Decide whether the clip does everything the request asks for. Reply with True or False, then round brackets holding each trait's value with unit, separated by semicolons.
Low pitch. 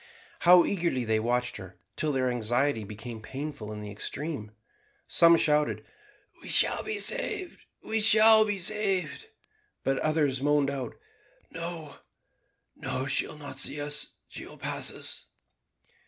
False (145 Hz)